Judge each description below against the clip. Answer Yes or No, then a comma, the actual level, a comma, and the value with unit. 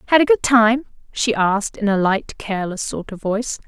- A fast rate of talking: Yes, fast, 215 wpm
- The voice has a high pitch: Yes, high, 220 Hz